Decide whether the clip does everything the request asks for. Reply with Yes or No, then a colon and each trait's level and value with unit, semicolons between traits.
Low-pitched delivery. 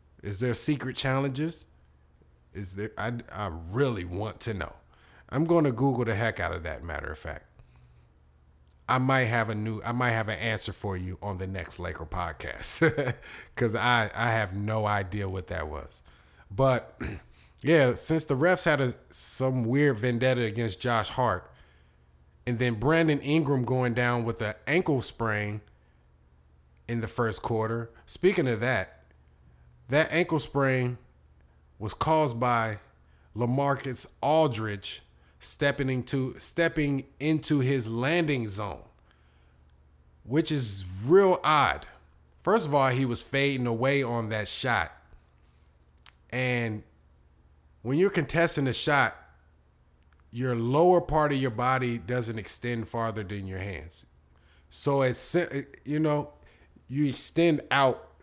Yes: low, 115 Hz